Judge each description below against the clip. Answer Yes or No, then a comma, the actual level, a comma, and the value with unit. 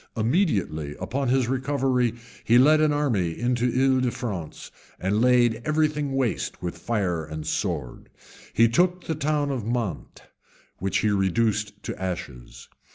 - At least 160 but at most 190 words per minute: No, average, 150 wpm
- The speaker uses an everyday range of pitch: No, wide, 5.7 semitones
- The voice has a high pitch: No, low, 120 Hz